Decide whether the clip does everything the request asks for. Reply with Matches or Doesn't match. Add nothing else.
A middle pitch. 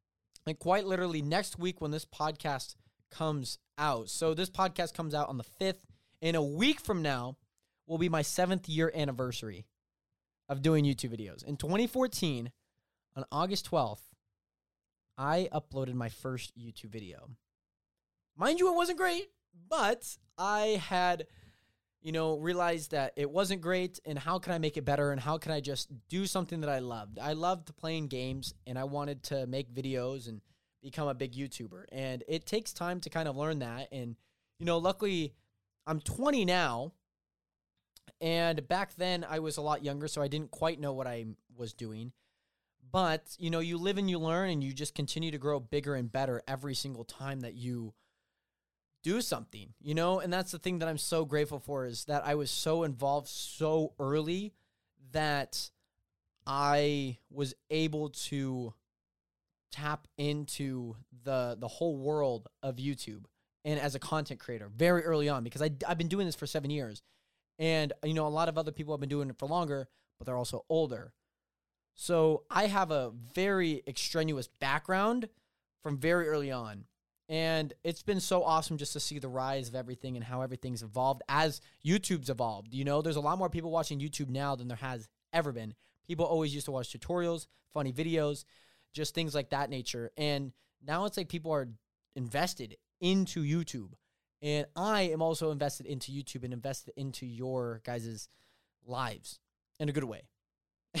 Matches